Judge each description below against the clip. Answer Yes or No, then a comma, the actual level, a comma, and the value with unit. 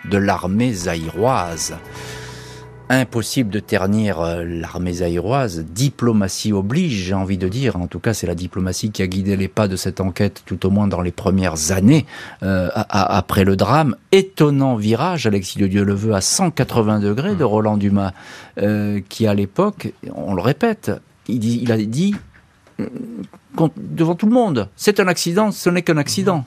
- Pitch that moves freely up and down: Yes, wide, 5.9 semitones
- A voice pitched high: No, low, 105 Hz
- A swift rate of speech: No, average, 175 wpm